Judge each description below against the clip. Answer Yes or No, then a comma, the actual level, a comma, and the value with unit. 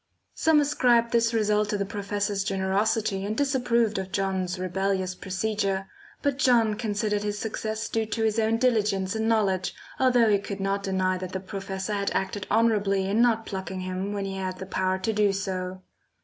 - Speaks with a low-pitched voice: No, high, 205 Hz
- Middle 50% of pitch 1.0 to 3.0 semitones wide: Yes, narrow, 2.6 semitones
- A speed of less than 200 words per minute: Yes, average, 180 wpm